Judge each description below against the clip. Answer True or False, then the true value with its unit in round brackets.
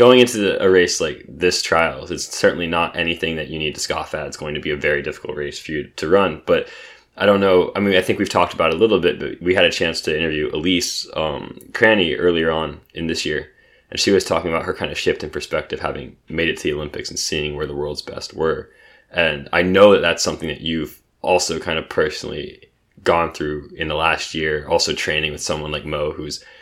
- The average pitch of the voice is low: True (80 Hz)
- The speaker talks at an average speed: False (245 wpm)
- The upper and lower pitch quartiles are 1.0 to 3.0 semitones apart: False (3.5 semitones)